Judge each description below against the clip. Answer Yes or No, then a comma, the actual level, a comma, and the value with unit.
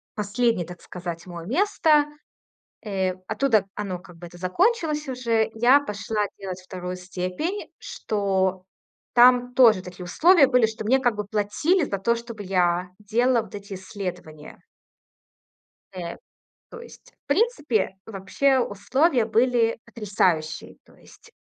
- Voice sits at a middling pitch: No, high, 215 Hz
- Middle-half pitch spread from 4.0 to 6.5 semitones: Yes, wide, 5.4 semitones